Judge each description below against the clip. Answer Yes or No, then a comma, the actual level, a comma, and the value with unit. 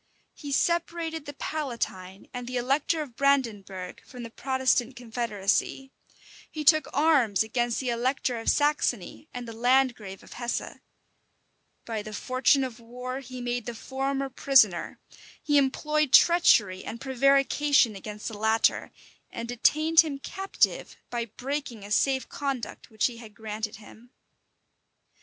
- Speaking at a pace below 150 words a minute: Yes, average, 140 wpm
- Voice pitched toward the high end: Yes, very high, 250 Hz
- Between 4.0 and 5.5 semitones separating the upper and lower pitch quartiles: No, average, 3.6 semitones